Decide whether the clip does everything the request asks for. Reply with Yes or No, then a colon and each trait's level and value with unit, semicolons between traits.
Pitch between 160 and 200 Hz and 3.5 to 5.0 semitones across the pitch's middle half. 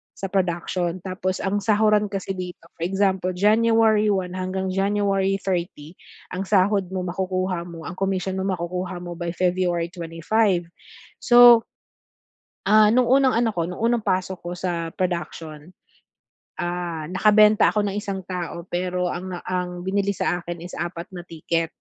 No: medium, 185 Hz; narrow, 2.4 semitones